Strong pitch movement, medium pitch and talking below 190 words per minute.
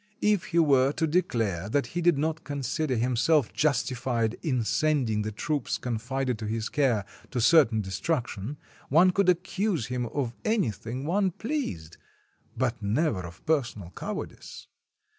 No: wide, 6.2 semitones; low, 130 Hz; average, 140 wpm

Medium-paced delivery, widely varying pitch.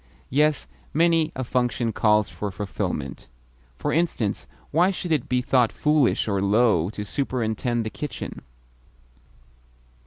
No: slow, 125 wpm; wide, 5.8 semitones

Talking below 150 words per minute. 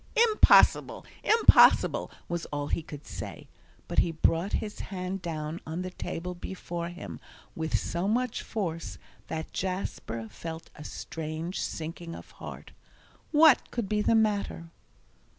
Yes: slow, 135 wpm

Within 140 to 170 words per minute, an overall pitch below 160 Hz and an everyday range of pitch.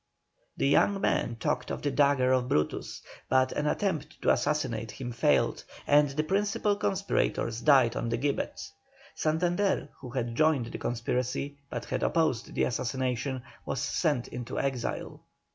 Yes: average, 150 wpm; low, 135 Hz; average, 3.9 semitones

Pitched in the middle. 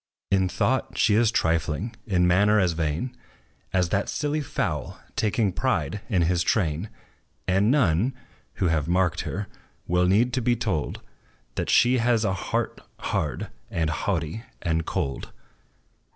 No: very low, 95 Hz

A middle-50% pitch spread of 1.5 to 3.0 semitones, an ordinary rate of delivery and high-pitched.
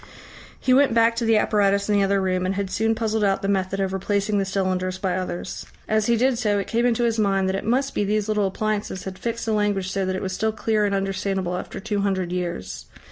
No: narrow, 2.4 semitones; fast, 250 wpm; high, 200 Hz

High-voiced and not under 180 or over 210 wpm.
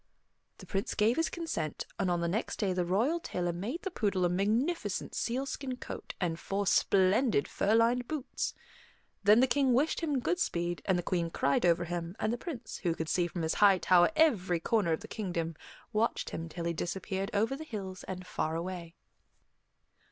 Yes: high, 195 Hz; average, 190 wpm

